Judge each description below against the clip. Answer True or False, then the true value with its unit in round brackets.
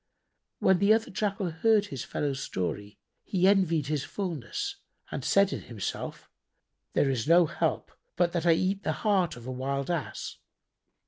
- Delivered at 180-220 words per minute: False (165 wpm)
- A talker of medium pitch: True (175 Hz)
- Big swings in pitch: True (6.3 semitones)